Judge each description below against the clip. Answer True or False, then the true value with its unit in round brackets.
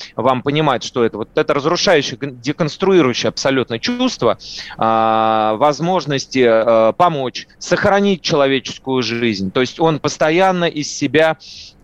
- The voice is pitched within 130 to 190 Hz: True (135 Hz)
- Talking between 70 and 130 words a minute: True (115 wpm)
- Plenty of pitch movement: True (6.0 semitones)